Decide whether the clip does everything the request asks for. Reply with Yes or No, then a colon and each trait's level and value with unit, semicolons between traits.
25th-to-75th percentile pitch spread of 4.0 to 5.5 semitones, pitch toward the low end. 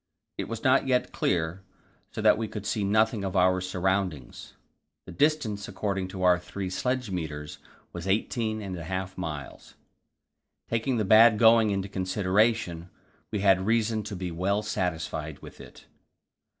No: average, 3.2 semitones; very low, 95 Hz